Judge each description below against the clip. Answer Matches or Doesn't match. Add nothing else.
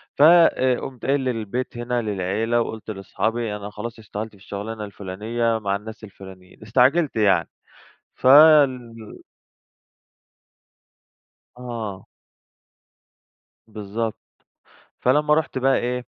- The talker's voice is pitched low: Matches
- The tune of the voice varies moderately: Matches